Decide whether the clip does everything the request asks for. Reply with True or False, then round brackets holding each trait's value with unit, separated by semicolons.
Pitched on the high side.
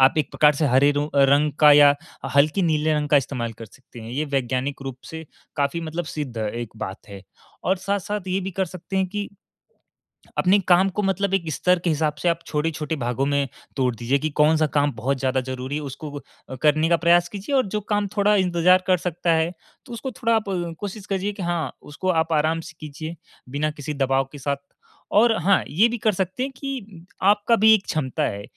False (155 Hz)